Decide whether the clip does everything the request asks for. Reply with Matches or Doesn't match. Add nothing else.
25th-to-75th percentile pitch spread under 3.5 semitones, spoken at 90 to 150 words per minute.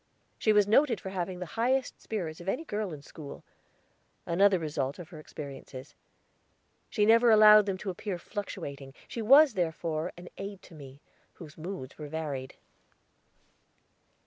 Doesn't match